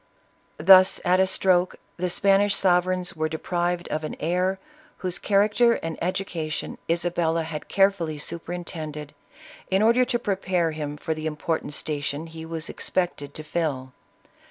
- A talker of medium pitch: Yes, medium, 175 Hz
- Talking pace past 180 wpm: No, average, 150 wpm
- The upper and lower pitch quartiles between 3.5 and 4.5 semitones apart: No, average, 3.0 semitones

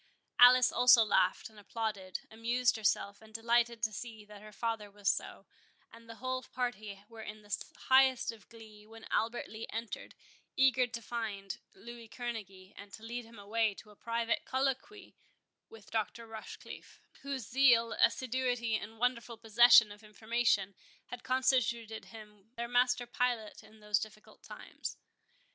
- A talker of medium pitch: No, high, 225 Hz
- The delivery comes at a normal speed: Yes, average, 150 wpm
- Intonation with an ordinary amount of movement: No, narrow, 2.3 semitones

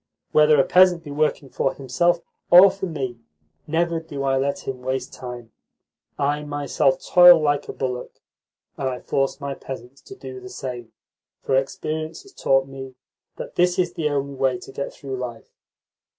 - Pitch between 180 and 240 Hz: No, medium, 140 Hz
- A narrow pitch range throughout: No, average, 3.7 semitones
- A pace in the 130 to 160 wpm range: No, average, 175 wpm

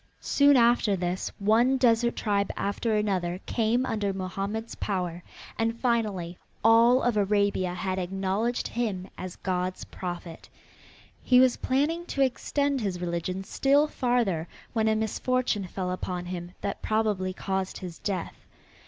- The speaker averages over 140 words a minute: No, slow, 135 wpm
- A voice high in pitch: Yes, high, 205 Hz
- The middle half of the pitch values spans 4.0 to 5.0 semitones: Yes, average, 4.3 semitones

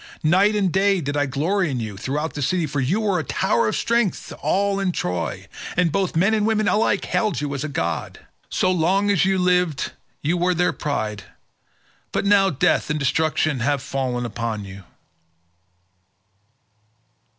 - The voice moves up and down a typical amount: No, wide, 6.1 semitones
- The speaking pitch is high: No, medium, 160 Hz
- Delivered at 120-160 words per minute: No, average, 175 wpm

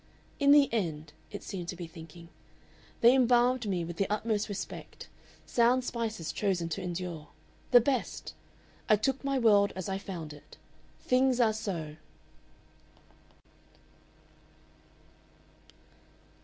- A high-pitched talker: Yes, high, 200 Hz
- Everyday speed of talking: No, slow, 120 wpm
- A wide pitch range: Yes, wide, 5.9 semitones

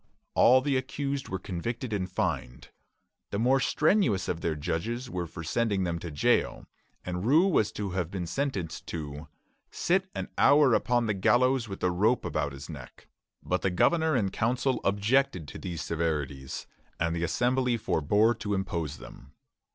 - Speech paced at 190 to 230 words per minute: No, average, 165 wpm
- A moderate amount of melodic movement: No, wide, 6.9 semitones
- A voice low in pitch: Yes, low, 100 Hz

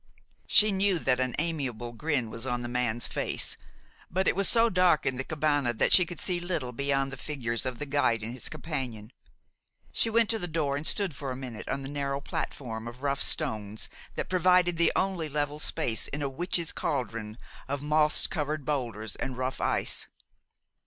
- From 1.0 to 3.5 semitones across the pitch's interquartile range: No, average, 4.7 semitones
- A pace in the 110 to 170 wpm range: No, average, 195 wpm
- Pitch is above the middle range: No, medium, 140 Hz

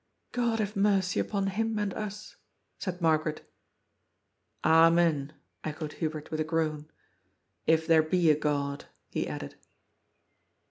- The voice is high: No, medium, 165 Hz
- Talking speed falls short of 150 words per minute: Yes, average, 140 wpm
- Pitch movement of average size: Yes, average, 4.2 semitones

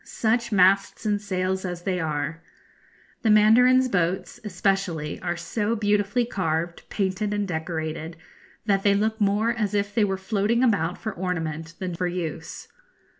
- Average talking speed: Yes, average, 150 wpm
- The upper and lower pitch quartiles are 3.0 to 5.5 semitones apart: Yes, average, 3.5 semitones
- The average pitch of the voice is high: Yes, high, 195 Hz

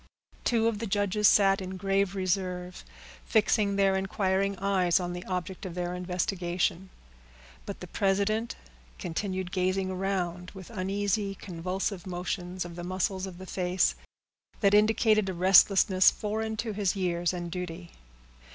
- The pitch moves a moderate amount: No, narrow, 1.8 semitones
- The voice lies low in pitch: No, high, 190 Hz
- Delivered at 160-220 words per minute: No, average, 140 wpm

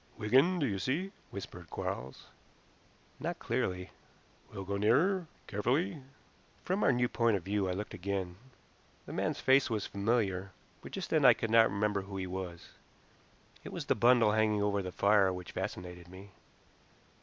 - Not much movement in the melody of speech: No, average, 4.5 semitones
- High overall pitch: No, low, 105 Hz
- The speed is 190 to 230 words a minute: No, average, 165 wpm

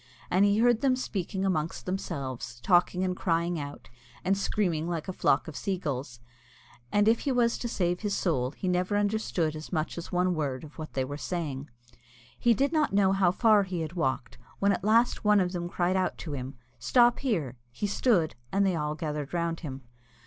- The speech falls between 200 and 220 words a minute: Yes, fast, 205 wpm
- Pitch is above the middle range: No, medium, 180 Hz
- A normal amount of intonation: Yes, average, 4.7 semitones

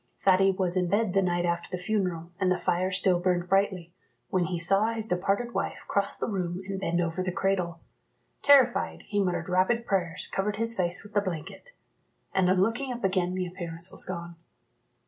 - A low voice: No, medium, 185 Hz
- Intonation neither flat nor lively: No, narrow, 2.2 semitones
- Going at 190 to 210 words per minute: Yes, average, 195 wpm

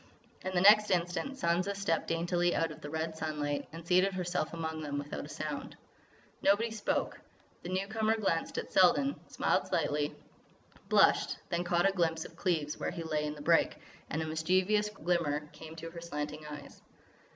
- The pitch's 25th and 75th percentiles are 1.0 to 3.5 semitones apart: Yes, average, 3.0 semitones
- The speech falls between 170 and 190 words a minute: Yes, average, 175 wpm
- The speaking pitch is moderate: Yes, medium, 170 Hz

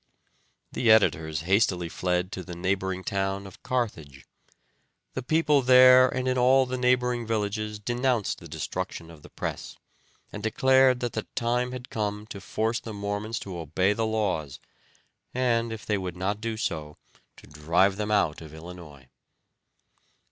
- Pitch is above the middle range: No, low, 105 Hz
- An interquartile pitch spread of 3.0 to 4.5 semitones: No, average, 5.2 semitones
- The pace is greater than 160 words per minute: No, average, 155 wpm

